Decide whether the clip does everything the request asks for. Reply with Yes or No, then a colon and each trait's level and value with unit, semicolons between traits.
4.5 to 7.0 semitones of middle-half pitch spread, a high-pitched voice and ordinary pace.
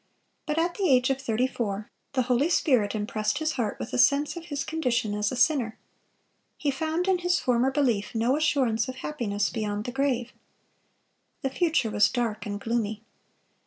Yes: average, 4.8 semitones; very high, 250 Hz; average, 180 wpm